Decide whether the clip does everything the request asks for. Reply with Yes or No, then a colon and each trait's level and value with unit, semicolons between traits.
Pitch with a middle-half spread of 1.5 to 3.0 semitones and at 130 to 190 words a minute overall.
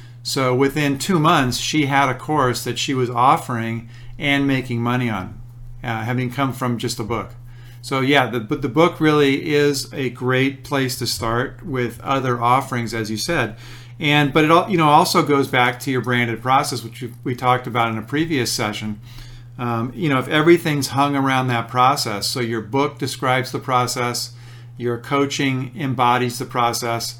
Yes: narrow, 2.5 semitones; average, 180 wpm